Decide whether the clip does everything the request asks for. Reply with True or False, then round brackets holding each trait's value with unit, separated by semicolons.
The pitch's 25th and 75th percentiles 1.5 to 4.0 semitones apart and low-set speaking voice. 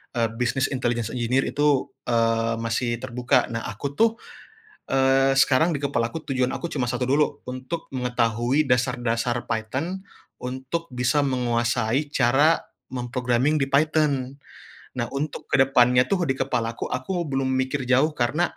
True (2.8 semitones; 130 Hz)